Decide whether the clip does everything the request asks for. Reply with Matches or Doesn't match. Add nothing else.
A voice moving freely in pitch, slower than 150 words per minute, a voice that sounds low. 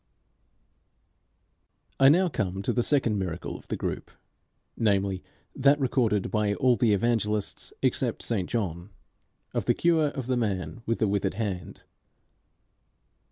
Doesn't match